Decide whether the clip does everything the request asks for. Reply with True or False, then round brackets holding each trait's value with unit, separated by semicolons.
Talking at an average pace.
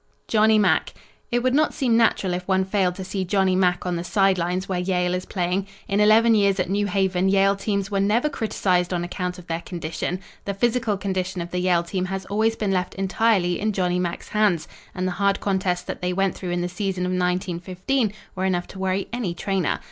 False (220 wpm)